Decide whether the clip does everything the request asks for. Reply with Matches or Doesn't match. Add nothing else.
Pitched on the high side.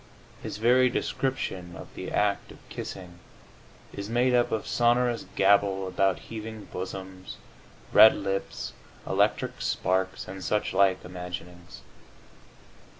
Doesn't match